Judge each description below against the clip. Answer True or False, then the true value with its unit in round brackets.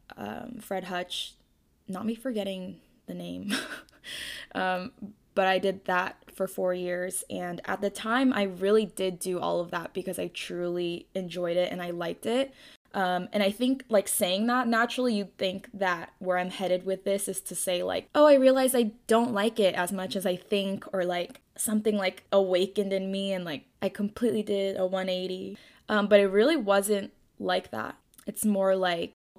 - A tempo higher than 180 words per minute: True (190 wpm)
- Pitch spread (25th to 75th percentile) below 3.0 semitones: True (2.6 semitones)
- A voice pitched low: False (195 Hz)